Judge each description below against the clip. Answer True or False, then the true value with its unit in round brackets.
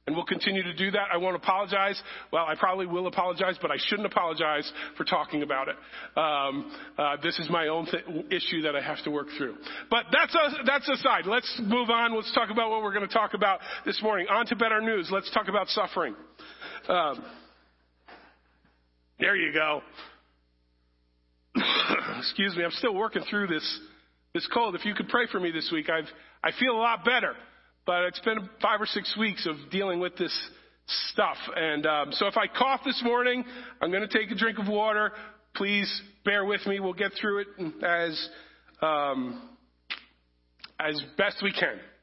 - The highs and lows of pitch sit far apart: True (5.7 semitones)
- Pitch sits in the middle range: False (195 Hz)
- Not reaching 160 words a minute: False (190 wpm)